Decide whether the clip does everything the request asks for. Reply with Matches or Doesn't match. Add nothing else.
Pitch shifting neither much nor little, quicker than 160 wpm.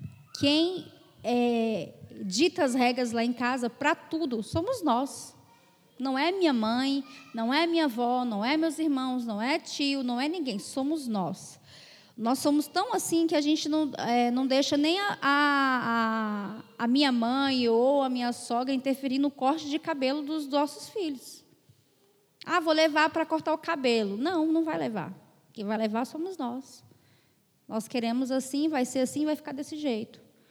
Matches